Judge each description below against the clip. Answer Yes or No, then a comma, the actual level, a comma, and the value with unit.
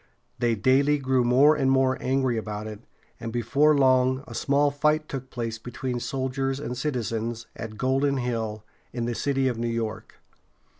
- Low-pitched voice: Yes, low, 130 Hz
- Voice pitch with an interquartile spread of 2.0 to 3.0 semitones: Yes, narrow, 2.6 semitones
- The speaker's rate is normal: Yes, average, 165 wpm